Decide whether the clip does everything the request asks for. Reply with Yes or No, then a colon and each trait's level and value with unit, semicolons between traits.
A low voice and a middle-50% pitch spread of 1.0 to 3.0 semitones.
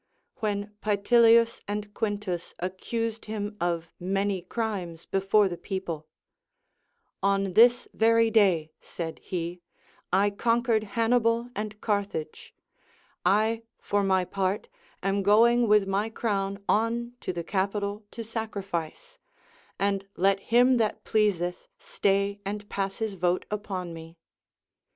No: high, 205 Hz; average, 2.7 semitones